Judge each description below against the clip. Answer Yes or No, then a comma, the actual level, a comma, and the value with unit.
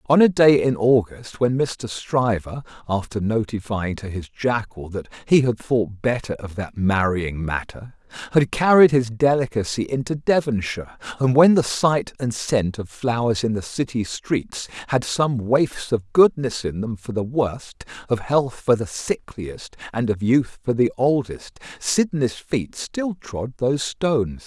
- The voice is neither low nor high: No, low, 120 Hz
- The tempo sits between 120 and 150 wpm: No, average, 165 wpm